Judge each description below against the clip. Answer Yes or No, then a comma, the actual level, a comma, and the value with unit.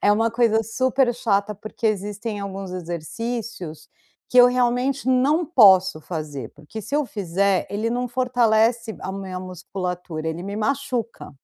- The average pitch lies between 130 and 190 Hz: No, high, 215 Hz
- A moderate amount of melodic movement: Yes, average, 4.6 semitones